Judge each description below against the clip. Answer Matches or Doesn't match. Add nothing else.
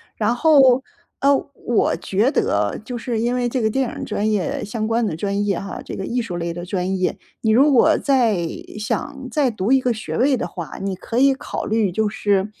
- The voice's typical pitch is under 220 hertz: Doesn't match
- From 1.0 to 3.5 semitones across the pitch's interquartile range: Doesn't match